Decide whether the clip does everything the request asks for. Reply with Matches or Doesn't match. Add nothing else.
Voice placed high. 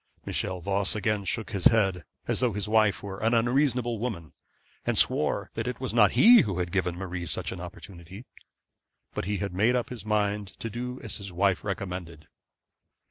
Doesn't match